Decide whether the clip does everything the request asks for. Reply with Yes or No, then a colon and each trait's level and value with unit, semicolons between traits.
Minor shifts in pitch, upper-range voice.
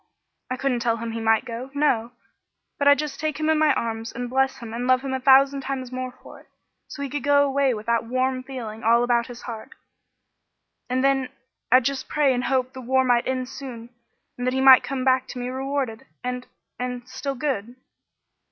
Yes: narrow, 2.0 semitones; very high, 255 Hz